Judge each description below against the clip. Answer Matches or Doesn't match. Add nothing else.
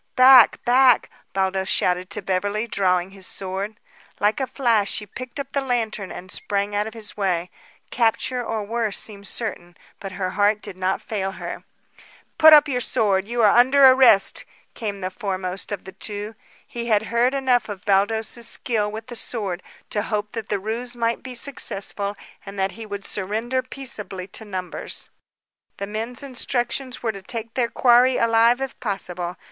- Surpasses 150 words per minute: Matches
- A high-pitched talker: Matches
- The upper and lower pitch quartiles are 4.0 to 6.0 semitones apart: Doesn't match